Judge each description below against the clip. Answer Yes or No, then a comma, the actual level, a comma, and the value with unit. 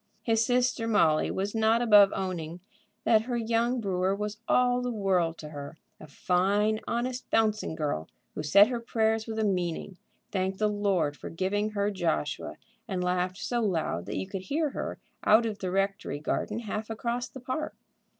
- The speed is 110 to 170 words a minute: No, average, 180 wpm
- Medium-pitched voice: No, high, 205 Hz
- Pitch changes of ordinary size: Yes, average, 3.9 semitones